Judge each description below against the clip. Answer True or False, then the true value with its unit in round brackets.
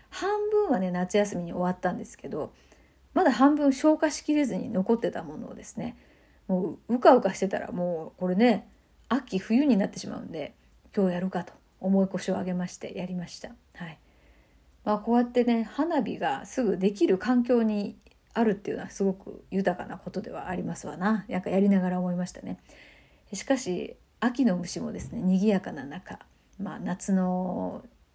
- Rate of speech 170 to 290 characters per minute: False (355 characters per minute)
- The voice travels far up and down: False (4.8 semitones)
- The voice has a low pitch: False (200 Hz)